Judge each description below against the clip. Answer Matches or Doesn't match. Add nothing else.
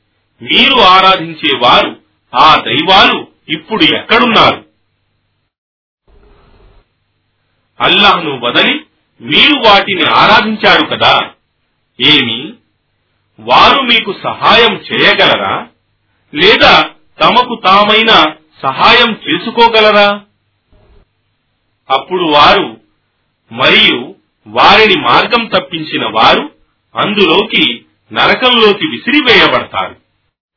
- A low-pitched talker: Doesn't match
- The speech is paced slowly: Matches